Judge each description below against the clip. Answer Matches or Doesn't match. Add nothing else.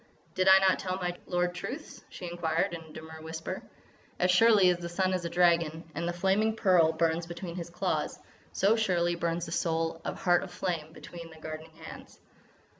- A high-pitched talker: Doesn't match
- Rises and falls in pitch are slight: Matches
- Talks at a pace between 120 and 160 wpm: Doesn't match